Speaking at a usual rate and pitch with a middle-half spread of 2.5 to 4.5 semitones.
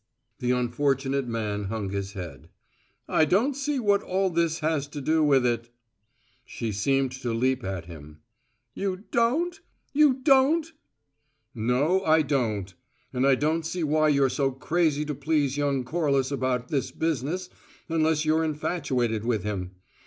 No: average, 155 wpm; average, 5.1 semitones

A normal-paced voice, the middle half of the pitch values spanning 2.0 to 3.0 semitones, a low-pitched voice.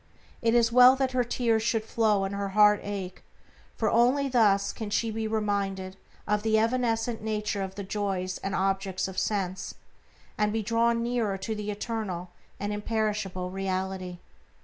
No: average, 165 wpm; average, 2.7 semitones; high, 210 Hz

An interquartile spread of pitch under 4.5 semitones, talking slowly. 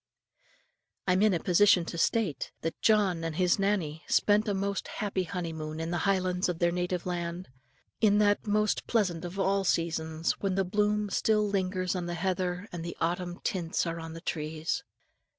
No: average, 3.0 semitones; average, 185 wpm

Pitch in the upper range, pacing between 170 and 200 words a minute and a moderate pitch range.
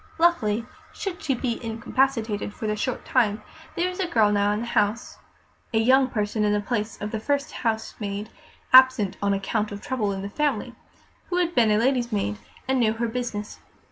Yes: high, 225 Hz; average, 190 wpm; average, 3.8 semitones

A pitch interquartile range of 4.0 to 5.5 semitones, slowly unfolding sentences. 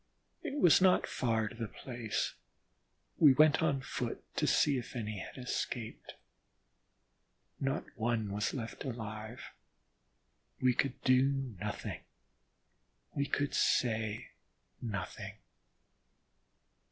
No: average, 3.5 semitones; slow, 105 wpm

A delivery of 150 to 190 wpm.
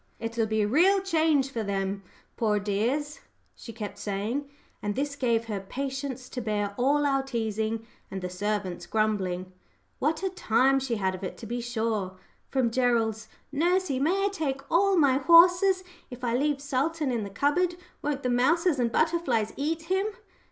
Yes: average, 175 wpm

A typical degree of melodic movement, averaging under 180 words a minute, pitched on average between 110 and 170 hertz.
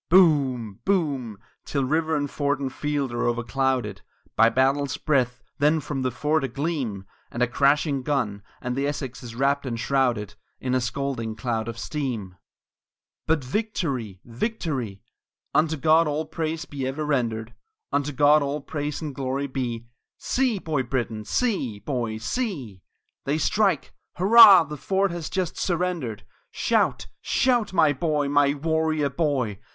Yes: average, 4.3 semitones; average, 155 wpm; medium, 140 Hz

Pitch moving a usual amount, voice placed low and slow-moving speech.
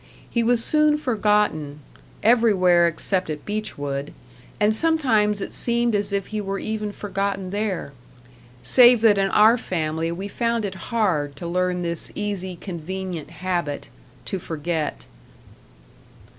No: average, 4.1 semitones; high, 195 Hz; slow, 130 wpm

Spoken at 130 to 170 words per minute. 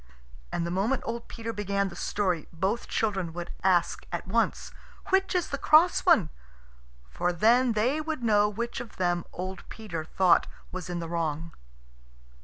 Yes: average, 165 wpm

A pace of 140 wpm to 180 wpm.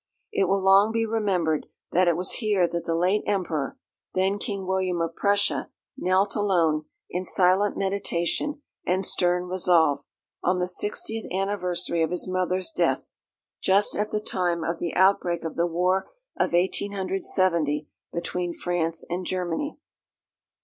Yes: average, 145 wpm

